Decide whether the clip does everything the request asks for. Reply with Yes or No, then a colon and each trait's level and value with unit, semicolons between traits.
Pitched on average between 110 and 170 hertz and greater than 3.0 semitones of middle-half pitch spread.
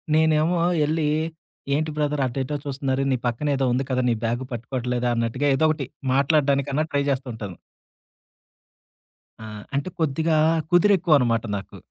Yes: medium, 140 Hz; average, 3.6 semitones